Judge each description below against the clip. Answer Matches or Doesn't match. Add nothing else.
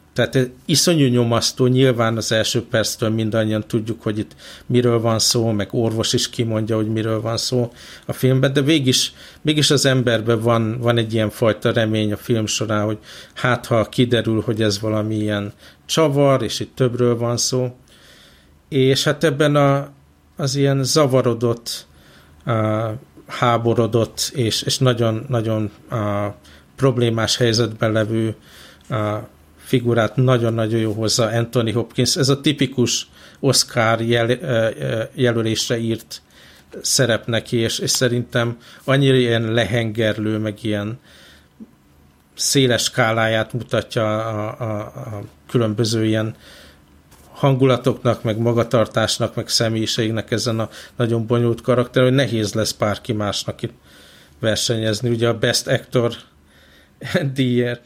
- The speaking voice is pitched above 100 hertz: Matches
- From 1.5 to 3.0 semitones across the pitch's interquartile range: Matches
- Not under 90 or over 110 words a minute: Doesn't match